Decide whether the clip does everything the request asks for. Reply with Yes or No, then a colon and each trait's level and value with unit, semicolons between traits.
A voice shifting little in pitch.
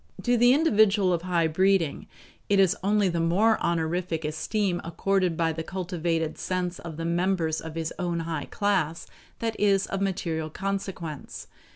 No: average, 3.1 semitones